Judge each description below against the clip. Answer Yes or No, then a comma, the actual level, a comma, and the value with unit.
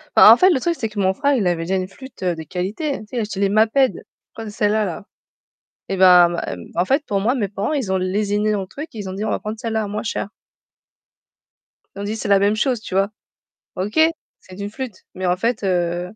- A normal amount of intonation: Yes, average, 3.0 semitones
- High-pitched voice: Yes, high, 205 Hz